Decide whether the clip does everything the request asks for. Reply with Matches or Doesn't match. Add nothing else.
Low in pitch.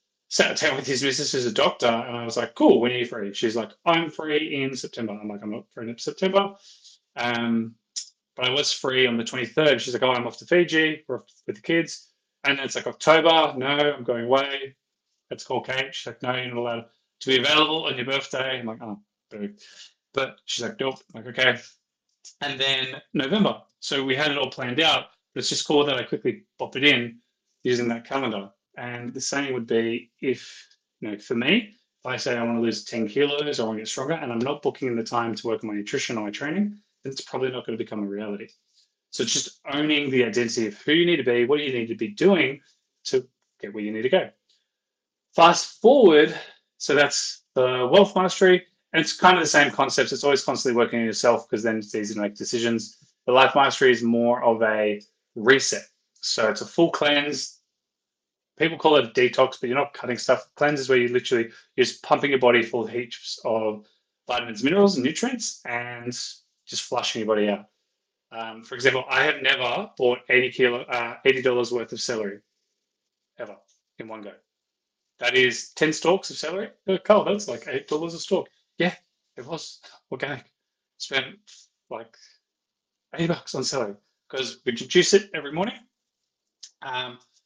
Matches